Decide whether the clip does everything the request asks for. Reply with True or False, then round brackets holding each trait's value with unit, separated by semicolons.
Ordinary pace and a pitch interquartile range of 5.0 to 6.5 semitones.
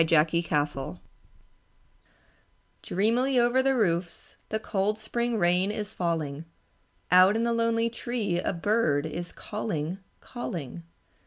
False (110 wpm; 5.5 semitones)